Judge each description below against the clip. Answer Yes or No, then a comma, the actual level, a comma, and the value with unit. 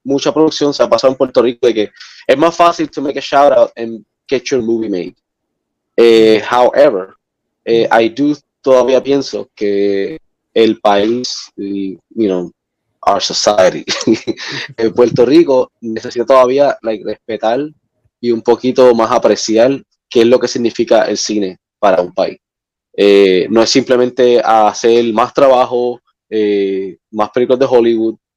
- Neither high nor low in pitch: No, low, 120 Hz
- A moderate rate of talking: Yes, average, 150 wpm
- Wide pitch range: No, average, 3.3 semitones